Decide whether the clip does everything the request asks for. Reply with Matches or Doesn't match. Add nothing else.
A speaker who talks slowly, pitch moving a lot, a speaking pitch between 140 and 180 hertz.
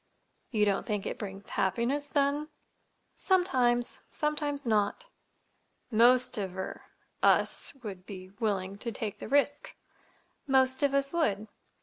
Doesn't match